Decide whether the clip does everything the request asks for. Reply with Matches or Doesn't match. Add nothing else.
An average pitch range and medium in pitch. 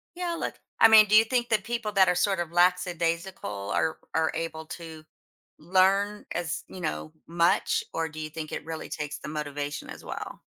Matches